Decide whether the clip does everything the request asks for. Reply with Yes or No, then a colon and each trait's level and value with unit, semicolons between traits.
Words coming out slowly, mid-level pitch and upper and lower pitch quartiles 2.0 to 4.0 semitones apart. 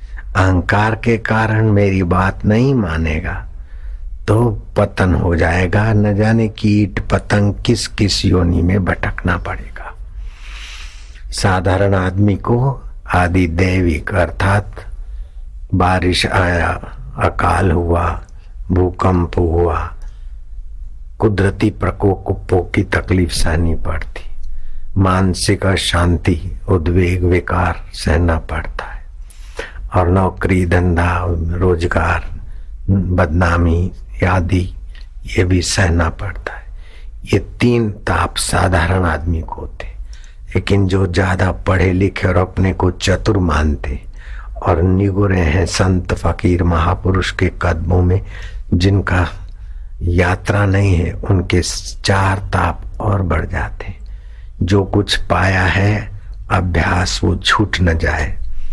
No: slow, 105 wpm; very low, 90 Hz; narrow, 2.5 semitones